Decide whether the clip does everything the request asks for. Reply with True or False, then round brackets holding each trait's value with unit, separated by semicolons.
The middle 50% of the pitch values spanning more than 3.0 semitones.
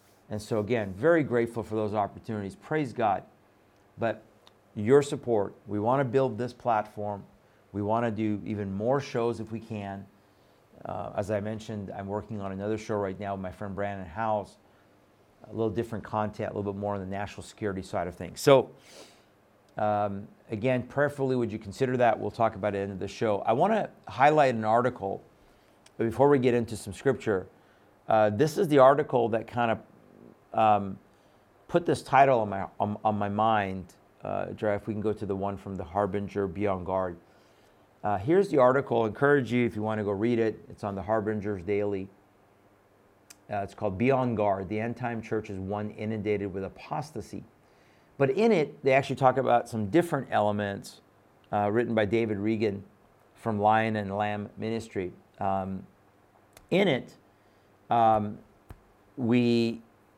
False (2.5 semitones)